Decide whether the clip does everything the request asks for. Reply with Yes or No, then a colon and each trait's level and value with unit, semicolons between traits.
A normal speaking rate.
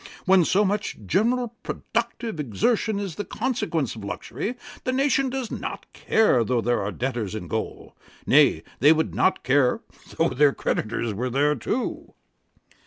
Yes: average, 155 wpm